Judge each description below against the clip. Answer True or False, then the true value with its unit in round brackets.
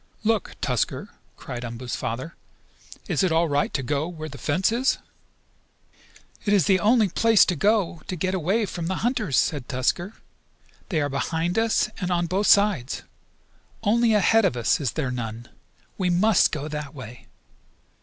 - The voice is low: False (175 Hz)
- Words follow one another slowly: False (170 wpm)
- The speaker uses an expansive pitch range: True (6.4 semitones)